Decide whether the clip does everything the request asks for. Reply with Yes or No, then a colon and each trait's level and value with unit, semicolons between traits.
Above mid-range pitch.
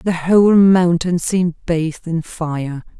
No: medium, 170 Hz